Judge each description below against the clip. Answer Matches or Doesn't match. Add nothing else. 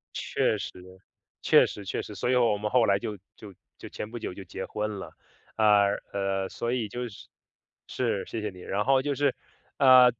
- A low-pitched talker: Matches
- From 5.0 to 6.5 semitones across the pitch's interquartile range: Doesn't match